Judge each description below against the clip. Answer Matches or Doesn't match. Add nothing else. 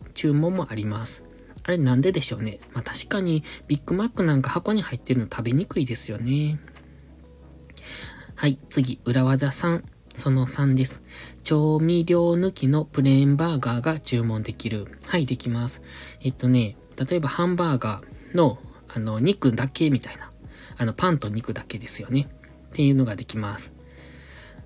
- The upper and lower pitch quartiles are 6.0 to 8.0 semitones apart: Doesn't match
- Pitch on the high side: Doesn't match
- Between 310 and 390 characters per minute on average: Matches